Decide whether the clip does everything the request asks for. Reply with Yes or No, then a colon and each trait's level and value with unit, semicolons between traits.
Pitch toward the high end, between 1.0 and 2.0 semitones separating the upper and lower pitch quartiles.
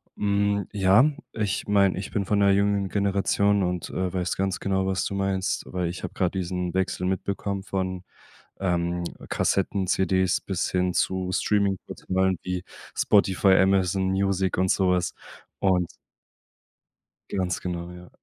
No: very low, 95 Hz; narrow, 1.3 semitones